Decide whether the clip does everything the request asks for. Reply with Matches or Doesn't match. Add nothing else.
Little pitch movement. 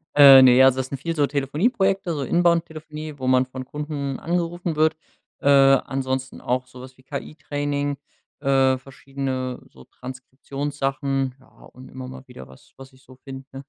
Matches